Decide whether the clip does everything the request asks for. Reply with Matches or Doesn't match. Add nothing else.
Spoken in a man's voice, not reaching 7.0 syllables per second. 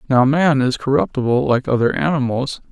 Matches